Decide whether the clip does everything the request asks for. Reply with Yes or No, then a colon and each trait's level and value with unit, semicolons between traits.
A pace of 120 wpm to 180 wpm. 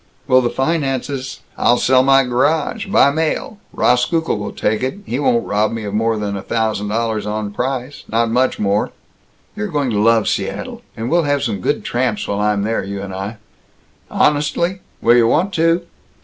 No: average, 190 wpm